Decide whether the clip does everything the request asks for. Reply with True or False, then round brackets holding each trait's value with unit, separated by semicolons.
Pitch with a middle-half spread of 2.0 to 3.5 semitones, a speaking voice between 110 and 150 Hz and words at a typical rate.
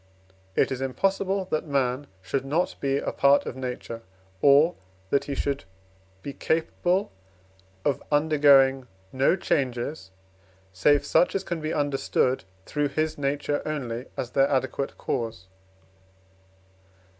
False (2.6 semitones; 140 Hz; 125 wpm)